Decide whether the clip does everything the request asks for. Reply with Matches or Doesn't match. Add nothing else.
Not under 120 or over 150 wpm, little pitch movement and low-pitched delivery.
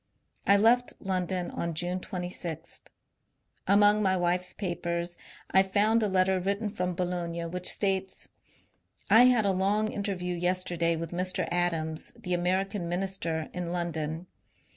Doesn't match